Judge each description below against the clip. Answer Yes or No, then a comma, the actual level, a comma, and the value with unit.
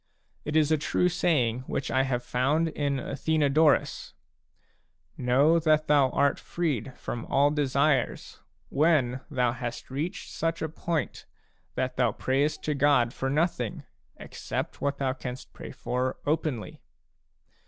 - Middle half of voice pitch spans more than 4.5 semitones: No, average, 3.3 semitones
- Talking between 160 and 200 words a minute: No, average, 145 wpm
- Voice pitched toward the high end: No, medium, 140 Hz